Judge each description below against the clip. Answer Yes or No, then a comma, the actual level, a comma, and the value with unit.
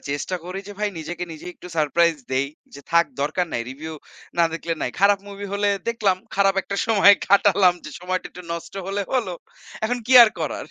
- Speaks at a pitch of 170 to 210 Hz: Yes, medium, 185 Hz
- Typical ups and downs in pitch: Yes, average, 3.3 semitones